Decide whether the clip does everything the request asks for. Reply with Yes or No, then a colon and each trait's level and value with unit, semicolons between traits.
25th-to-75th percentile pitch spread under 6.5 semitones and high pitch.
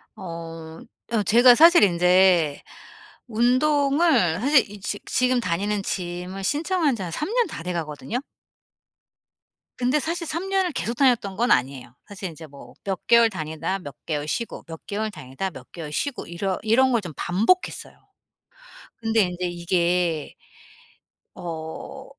No: wide, 6.8 semitones; high, 195 Hz